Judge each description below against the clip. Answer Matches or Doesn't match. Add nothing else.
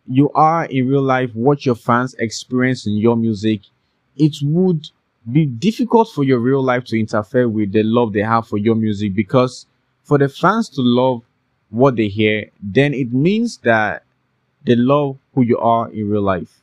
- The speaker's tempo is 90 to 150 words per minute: Doesn't match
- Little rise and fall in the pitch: Doesn't match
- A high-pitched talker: Doesn't match